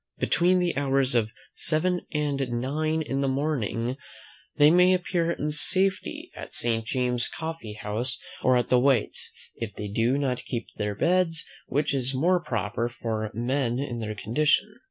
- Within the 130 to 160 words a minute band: Yes, average, 155 wpm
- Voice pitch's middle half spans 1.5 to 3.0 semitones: No, average, 5.0 semitones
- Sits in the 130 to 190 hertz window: Yes, low, 135 Hz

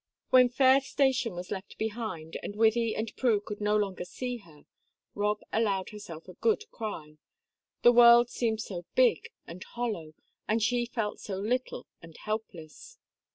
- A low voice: No, high, 215 Hz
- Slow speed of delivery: No, average, 155 wpm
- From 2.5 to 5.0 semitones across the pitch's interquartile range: Yes, average, 4.2 semitones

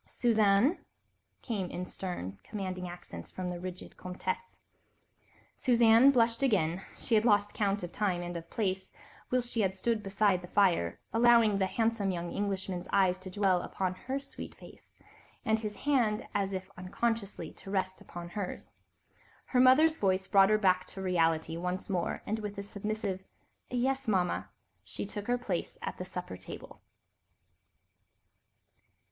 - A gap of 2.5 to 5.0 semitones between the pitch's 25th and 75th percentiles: Yes, average, 3.5 semitones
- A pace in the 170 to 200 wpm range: No, average, 155 wpm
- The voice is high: Yes, high, 195 Hz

